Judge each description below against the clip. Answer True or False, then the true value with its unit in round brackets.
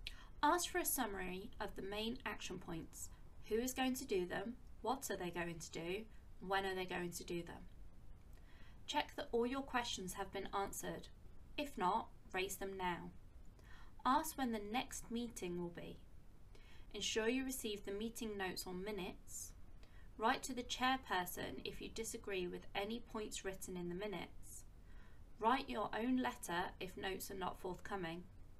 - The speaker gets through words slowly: False (165 wpm)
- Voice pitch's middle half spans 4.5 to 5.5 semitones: True (4.8 semitones)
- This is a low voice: False (195 Hz)